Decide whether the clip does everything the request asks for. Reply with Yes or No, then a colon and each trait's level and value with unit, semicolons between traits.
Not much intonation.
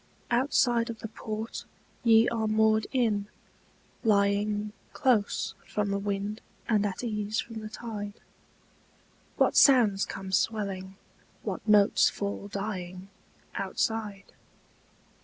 Yes: narrow, 1.9 semitones